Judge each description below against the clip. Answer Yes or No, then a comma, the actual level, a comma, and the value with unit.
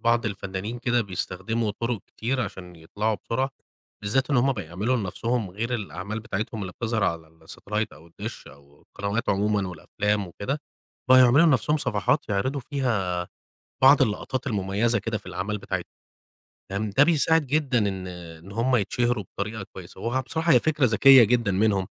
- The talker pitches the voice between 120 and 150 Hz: No, low, 110 Hz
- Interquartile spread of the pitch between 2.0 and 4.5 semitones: Yes, average, 4.2 semitones